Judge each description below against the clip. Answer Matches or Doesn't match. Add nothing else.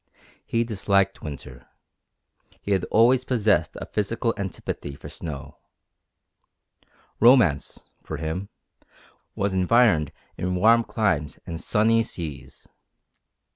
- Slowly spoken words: Matches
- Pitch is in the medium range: Doesn't match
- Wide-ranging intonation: Matches